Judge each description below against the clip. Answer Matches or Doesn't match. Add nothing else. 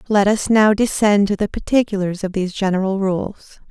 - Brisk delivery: Doesn't match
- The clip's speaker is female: Matches